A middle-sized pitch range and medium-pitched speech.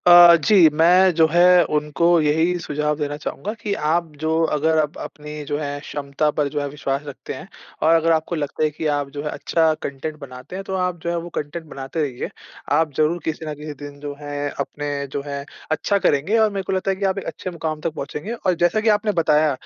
Yes: average, 3.0 semitones; medium, 155 Hz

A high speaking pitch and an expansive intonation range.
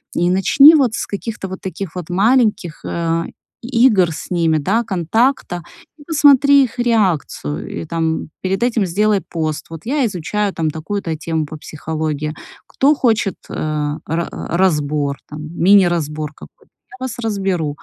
No: medium, 180 Hz; wide, 5.9 semitones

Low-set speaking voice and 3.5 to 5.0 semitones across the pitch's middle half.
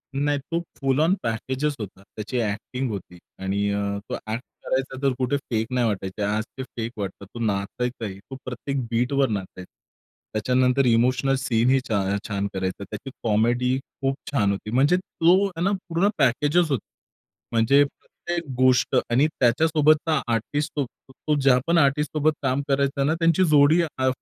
Yes: low, 130 Hz; average, 4.4 semitones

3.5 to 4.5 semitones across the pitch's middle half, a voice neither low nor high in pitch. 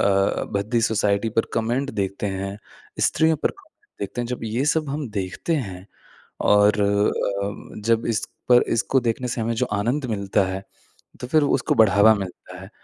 No: average, 3.8 semitones; low, 110 Hz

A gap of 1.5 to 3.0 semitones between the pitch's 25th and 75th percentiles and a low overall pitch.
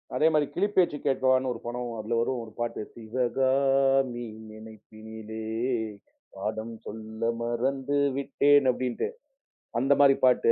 No: average, 3.4 semitones; low, 125 Hz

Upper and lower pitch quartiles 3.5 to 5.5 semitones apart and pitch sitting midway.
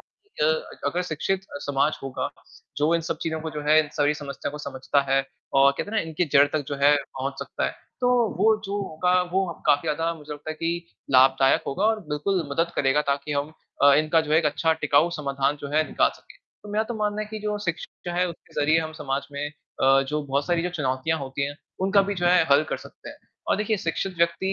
Yes: average, 4.1 semitones; medium, 155 Hz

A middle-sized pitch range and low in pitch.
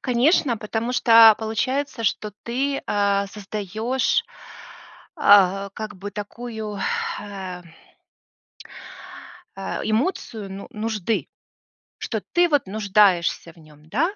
No: average, 3.0 semitones; high, 215 Hz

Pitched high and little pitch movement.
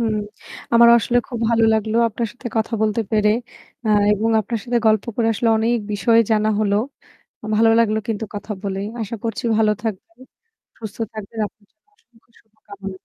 Yes: high, 220 Hz; narrow, 1.6 semitones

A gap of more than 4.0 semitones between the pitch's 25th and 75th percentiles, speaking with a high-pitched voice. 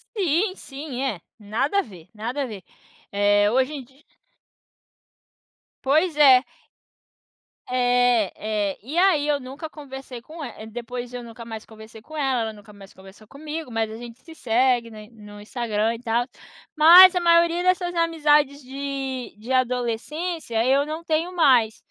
Yes: average, 5.2 semitones; very high, 255 Hz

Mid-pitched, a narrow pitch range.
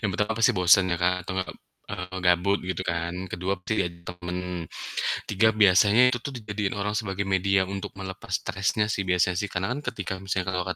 No: very low, 95 Hz; narrow, 2.2 semitones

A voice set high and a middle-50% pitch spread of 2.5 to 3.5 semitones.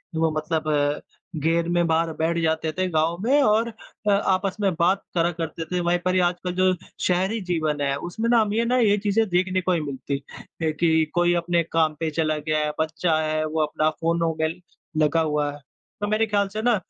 No: medium, 170 Hz; average, 3.1 semitones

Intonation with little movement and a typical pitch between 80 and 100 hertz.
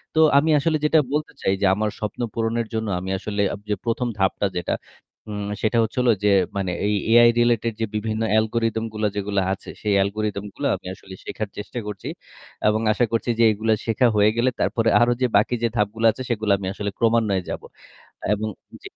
No: narrow, 2.2 semitones; low, 110 Hz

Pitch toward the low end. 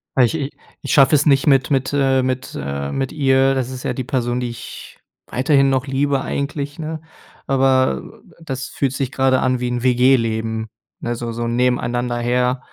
Yes: low, 130 Hz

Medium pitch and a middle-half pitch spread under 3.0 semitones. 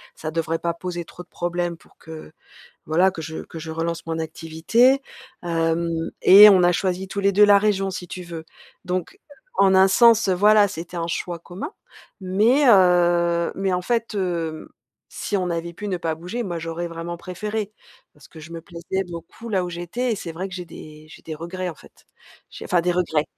Yes: medium, 175 Hz; narrow, 2.6 semitones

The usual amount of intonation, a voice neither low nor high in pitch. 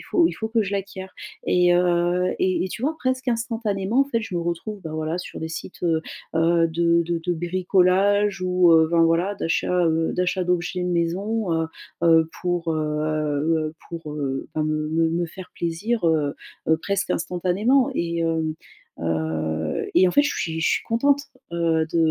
Yes: average, 3.0 semitones; medium, 175 Hz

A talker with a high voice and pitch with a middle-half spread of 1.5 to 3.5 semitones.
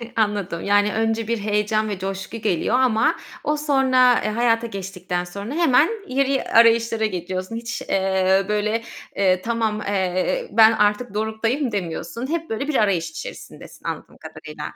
Yes: high, 220 Hz; average, 3.2 semitones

